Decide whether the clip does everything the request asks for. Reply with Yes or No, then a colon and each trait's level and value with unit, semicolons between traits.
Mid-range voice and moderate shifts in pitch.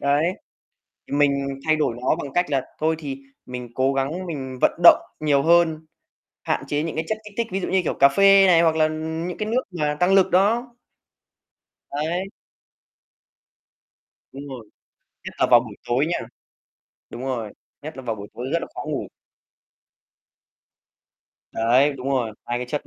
Yes: medium, 150 Hz; average, 4.3 semitones